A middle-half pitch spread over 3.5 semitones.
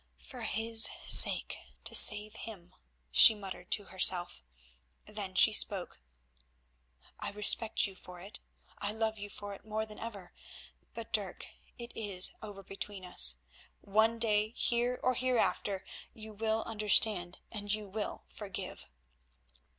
No: average, 2.7 semitones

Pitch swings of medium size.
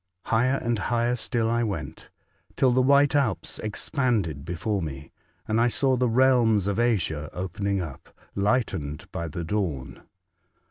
No: wide, 6.2 semitones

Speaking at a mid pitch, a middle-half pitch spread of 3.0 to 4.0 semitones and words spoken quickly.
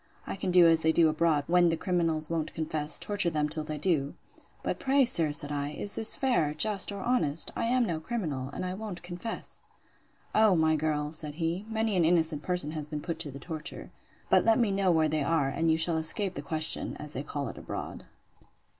Yes: medium, 165 Hz; average, 3.5 semitones; fast, 215 wpm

